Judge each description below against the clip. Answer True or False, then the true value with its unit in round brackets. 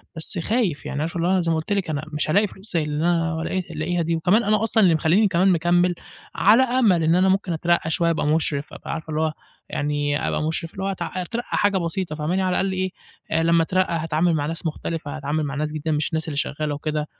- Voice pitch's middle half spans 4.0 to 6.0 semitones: False (3.2 semitones)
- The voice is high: False (165 Hz)